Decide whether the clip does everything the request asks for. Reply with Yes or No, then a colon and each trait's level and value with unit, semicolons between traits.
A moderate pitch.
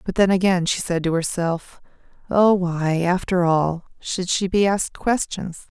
Yes: medium, 180 Hz